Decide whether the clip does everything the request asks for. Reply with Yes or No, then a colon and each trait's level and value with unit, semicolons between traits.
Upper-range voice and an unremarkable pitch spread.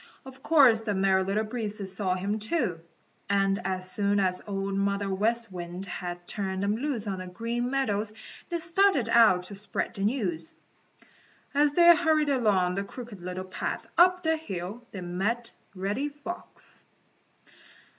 Yes: high, 205 Hz; average, 4.8 semitones